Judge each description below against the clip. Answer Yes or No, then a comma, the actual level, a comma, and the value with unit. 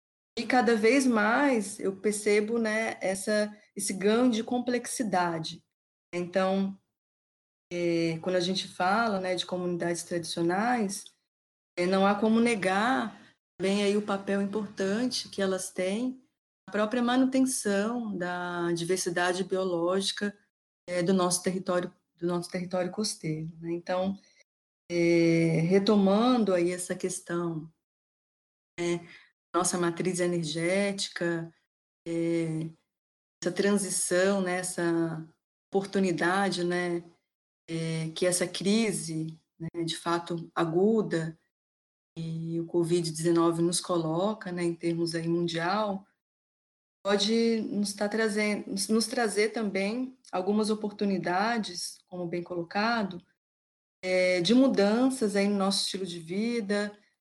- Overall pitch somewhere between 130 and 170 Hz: No, medium, 185 Hz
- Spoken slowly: Yes, slow, 110 wpm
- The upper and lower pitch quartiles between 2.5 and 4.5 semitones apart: Yes, average, 3.4 semitones